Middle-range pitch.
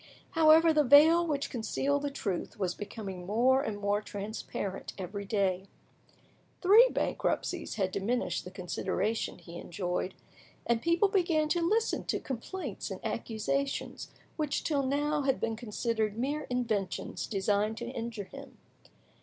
No: high, 235 Hz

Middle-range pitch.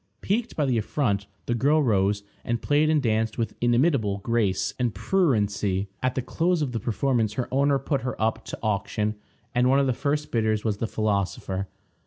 No: low, 120 Hz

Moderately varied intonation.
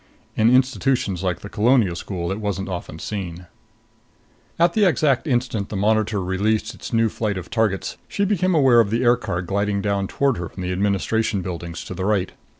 Yes: average, 4.3 semitones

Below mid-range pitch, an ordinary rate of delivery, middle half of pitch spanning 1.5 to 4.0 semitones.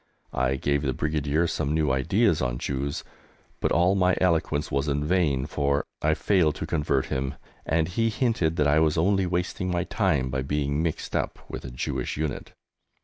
Yes: very low, 75 Hz; average, 185 wpm; average, 3.6 semitones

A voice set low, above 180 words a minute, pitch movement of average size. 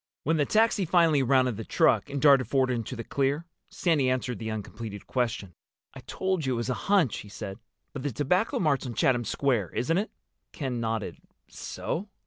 Yes: low, 130 Hz; average, 190 wpm; average, 4.7 semitones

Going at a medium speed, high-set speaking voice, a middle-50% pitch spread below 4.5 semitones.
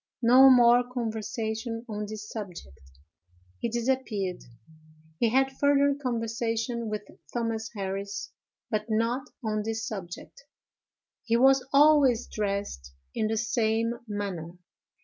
No: slow, 110 wpm; high, 225 Hz; average, 2.8 semitones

